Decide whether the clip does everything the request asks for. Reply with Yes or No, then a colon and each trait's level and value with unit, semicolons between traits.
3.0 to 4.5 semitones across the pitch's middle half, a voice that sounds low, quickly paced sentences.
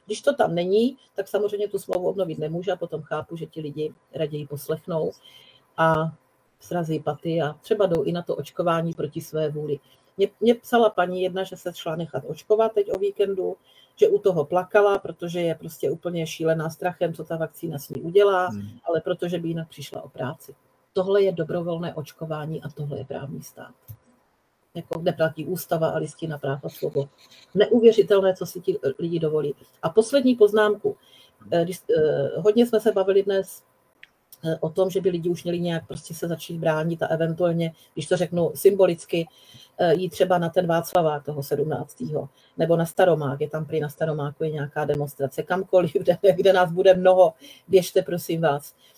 No: average, 3.4 semitones; medium, 170 Hz; fast, 175 wpm